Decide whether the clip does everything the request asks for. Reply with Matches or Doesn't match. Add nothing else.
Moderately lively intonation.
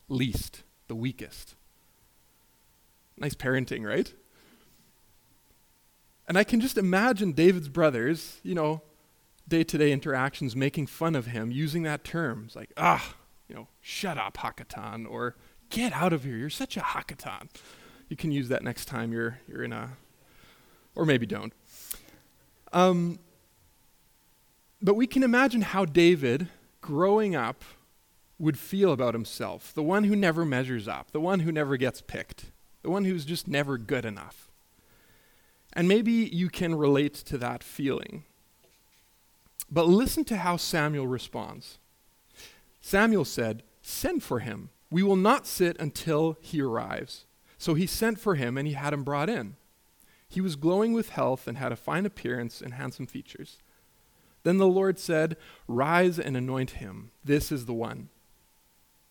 Doesn't match